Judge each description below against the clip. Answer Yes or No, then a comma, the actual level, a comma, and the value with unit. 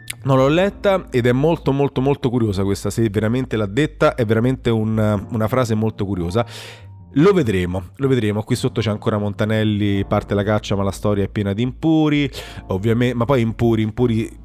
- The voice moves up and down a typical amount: Yes, average, 3.8 semitones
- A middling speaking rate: No, fast, 185 wpm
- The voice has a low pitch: Yes, low, 115 Hz